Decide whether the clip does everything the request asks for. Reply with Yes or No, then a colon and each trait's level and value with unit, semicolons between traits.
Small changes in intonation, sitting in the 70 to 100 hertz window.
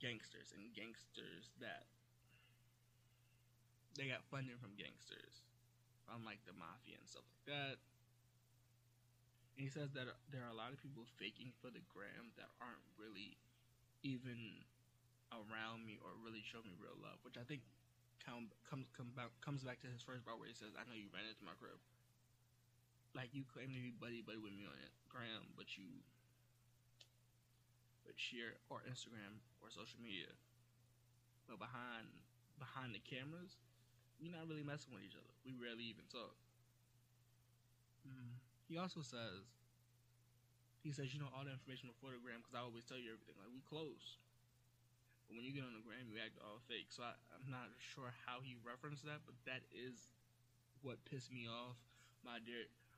No: narrow, 1.1 semitones; low, 120 Hz